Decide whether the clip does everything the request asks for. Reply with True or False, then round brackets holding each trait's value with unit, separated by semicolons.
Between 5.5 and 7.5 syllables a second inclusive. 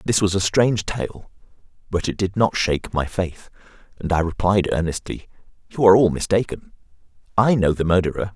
True (5.6 syllables/s)